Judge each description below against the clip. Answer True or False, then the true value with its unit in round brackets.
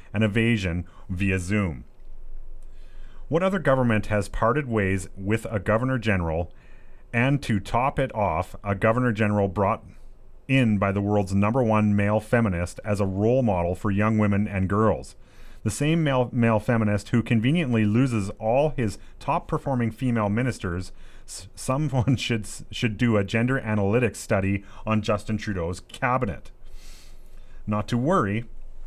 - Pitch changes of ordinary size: True (3.4 semitones)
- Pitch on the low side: True (110 Hz)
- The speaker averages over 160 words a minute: False (150 wpm)